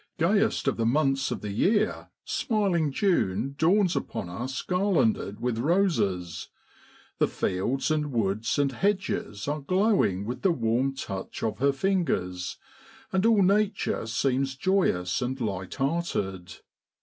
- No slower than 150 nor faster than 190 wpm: No, slow, 135 wpm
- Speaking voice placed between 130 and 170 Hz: Yes, low, 135 Hz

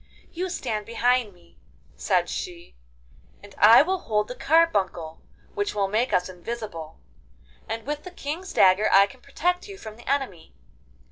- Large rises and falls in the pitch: Yes, wide, 7.4 semitones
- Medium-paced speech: Yes, average, 155 wpm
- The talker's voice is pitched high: Yes, high, 225 Hz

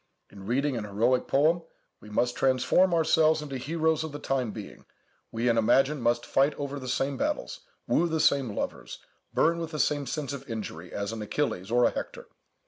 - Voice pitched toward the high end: No, low, 135 Hz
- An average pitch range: Yes, average, 4.7 semitones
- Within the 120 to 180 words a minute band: No, average, 195 wpm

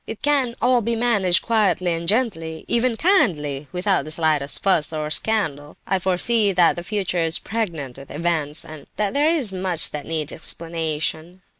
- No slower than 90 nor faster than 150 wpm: No, average, 175 wpm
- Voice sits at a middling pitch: Yes, medium, 175 Hz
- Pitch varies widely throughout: Yes, wide, 5.8 semitones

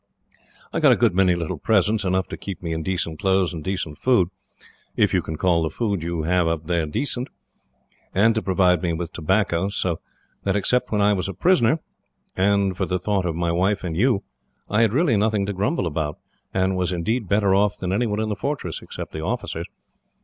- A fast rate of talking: Yes, fast, 210 wpm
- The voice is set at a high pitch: No, very low, 95 Hz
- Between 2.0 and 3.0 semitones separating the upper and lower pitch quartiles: No, average, 3.4 semitones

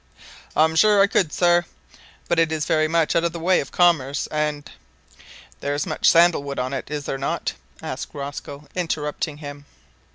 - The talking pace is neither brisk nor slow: Yes, average, 190 wpm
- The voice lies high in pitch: No, medium, 155 Hz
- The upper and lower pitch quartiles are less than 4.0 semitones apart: Yes, average, 3.0 semitones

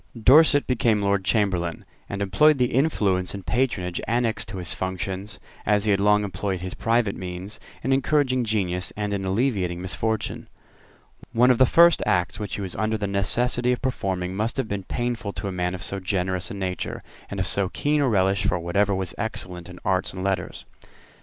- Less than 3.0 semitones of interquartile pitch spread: No, average, 3.9 semitones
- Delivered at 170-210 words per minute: Yes, average, 190 wpm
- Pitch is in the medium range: No, low, 100 Hz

